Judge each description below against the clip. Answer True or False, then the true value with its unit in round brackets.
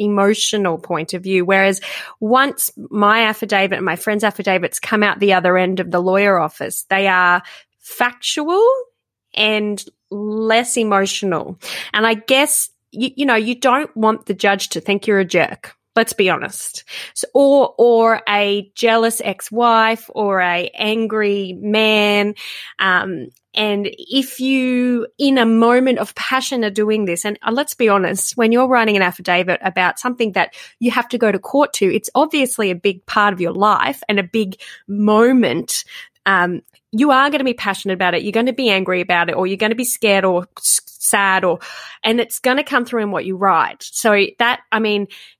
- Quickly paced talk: False (185 wpm)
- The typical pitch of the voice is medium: False (215 Hz)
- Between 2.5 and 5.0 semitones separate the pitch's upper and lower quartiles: True (3.9 semitones)